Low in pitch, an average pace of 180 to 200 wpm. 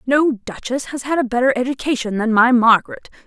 No: very high, 250 Hz; average, 185 wpm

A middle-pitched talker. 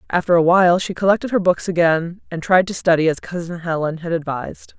Yes: medium, 170 Hz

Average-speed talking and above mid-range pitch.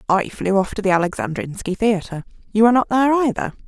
Yes: average, 195 wpm; high, 205 Hz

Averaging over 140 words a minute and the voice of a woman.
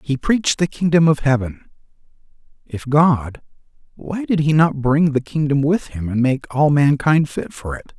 No: average, 180 wpm; male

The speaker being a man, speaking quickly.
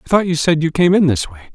Yes: male; fast, 350 wpm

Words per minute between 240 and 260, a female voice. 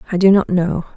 Yes: fast, 250 wpm; female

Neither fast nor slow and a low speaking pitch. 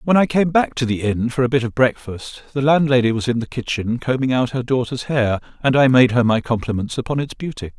No: fast, 245 wpm; low, 125 Hz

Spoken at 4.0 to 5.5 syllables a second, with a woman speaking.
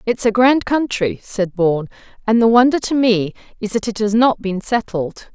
Yes: 4.8 syllables/s; female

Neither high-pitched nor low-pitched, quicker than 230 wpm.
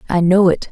Yes: medium, 180 Hz; fast, 250 wpm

